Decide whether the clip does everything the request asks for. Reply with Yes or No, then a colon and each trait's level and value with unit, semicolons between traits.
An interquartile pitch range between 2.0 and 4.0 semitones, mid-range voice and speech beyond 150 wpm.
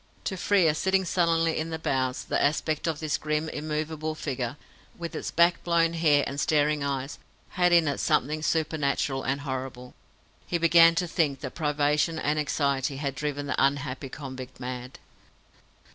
Yes: average, 3.0 semitones; medium, 150 Hz; average, 160 wpm